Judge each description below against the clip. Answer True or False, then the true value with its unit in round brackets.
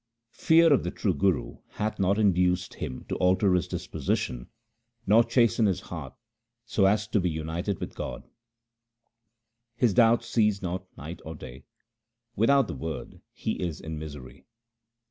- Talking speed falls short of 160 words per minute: True (150 wpm)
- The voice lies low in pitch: True (95 Hz)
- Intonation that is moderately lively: True (5.0 semitones)